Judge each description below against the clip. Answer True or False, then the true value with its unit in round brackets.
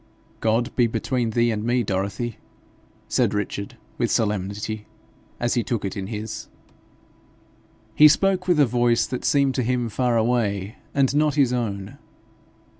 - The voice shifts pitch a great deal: False (3.3 semitones)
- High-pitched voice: False (120 Hz)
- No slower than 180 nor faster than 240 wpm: False (150 wpm)